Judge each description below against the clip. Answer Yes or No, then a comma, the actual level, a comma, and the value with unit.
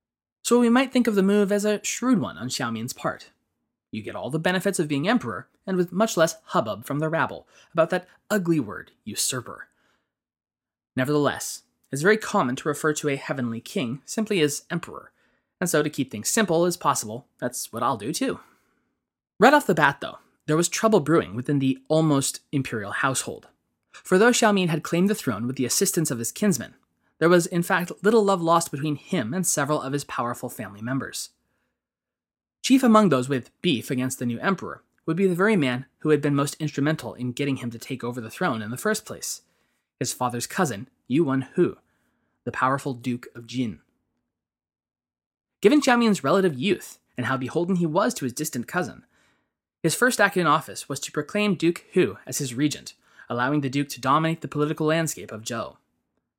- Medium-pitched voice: Yes, medium, 150 Hz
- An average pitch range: No, wide, 6.1 semitones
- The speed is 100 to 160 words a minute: No, average, 195 wpm